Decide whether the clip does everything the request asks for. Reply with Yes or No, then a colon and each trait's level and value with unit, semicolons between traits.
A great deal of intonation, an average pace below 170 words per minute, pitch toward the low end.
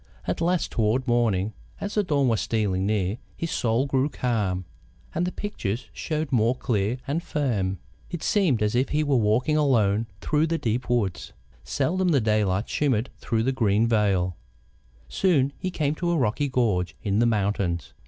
No: wide, 5.7 semitones; average, 175 wpm; low, 120 Hz